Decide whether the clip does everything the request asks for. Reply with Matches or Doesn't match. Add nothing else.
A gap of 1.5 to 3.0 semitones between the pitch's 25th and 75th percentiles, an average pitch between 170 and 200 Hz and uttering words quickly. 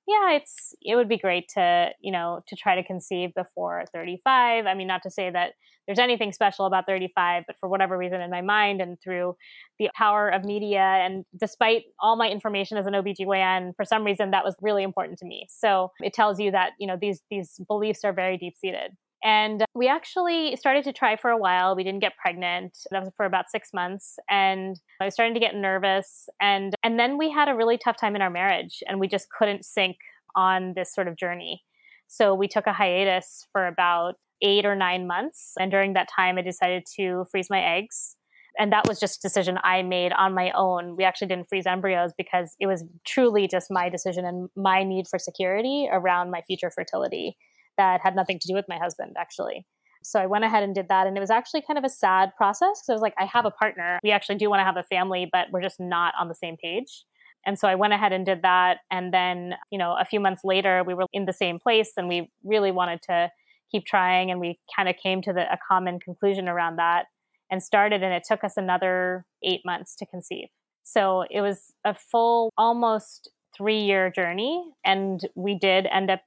Matches